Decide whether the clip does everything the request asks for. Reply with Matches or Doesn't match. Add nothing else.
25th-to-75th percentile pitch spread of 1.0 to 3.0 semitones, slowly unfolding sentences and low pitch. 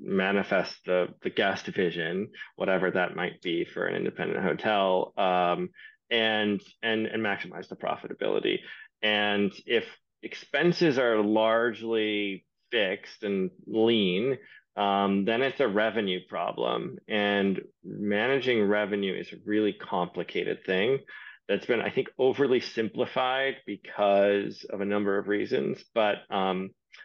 Matches